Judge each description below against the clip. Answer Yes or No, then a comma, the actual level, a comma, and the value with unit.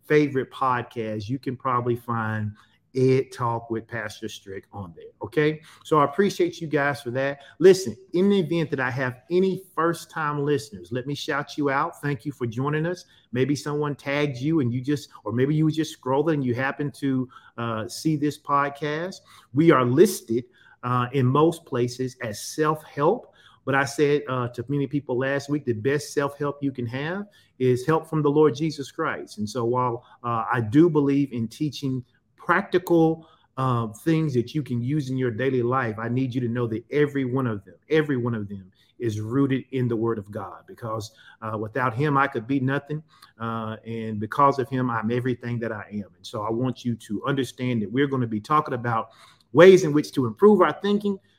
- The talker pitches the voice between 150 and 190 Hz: No, low, 135 Hz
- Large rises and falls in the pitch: No, average, 4.0 semitones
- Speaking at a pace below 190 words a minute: No, fast, 205 wpm